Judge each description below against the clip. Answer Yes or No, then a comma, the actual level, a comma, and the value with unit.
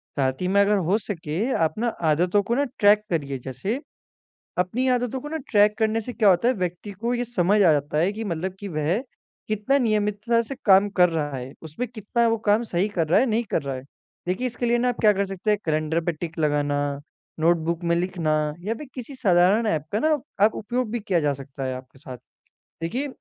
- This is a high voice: Yes, high, 195 Hz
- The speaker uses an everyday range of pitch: No, wide, 6.1 semitones